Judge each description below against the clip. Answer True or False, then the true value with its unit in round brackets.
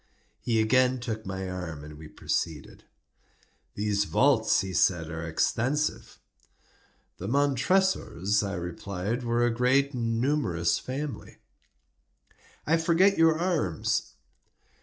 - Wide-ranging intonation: True (7.2 semitones)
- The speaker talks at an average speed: False (115 wpm)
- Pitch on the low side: True (115 Hz)